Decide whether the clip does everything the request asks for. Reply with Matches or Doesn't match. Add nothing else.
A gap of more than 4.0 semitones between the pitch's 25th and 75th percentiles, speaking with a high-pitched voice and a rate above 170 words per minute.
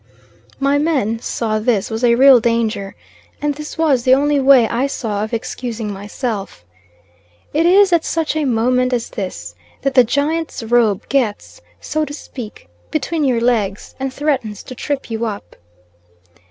Doesn't match